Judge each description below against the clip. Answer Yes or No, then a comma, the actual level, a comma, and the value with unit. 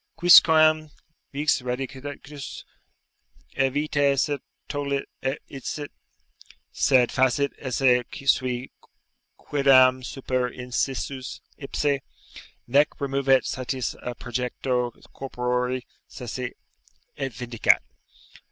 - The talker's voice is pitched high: No, low, 135 Hz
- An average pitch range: No, narrow, 2.1 semitones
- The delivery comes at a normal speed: No, slow, 85 wpm